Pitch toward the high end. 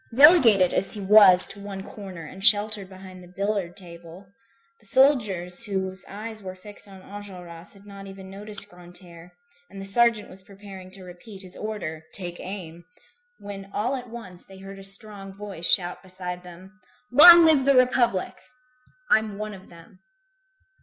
Yes: high, 195 Hz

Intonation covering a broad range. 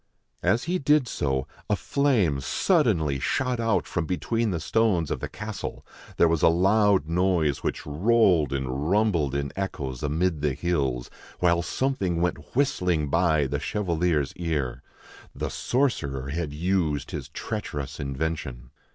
Yes: wide, 5.7 semitones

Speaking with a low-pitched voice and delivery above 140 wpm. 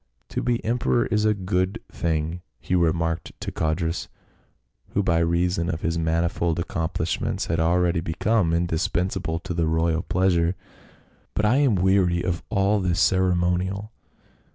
Yes: very low, 90 Hz; average, 150 wpm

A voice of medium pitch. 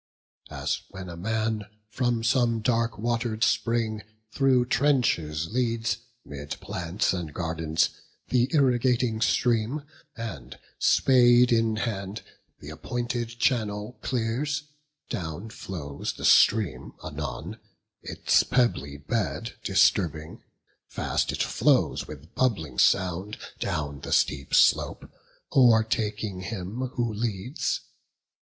No: low, 110 Hz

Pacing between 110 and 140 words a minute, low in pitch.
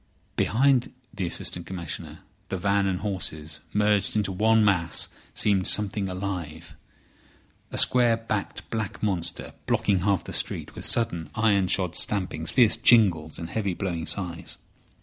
Yes: slow, 135 wpm; very low, 95 Hz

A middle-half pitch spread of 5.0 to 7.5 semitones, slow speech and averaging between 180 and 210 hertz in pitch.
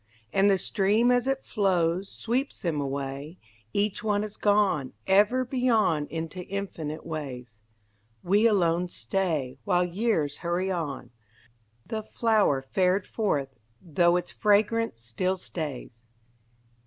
Yes: wide, 5.4 semitones; slow, 120 wpm; medium, 185 Hz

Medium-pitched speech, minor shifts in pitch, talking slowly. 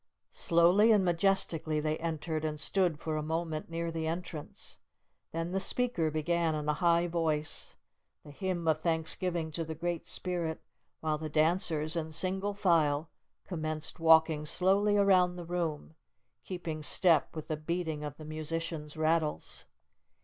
No: medium, 165 Hz; narrow, 2.1 semitones; average, 150 wpm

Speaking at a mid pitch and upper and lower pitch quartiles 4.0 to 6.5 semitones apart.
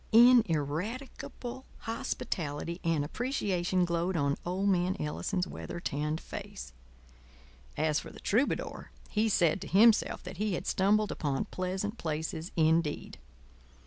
Yes: medium, 180 Hz; average, 4.7 semitones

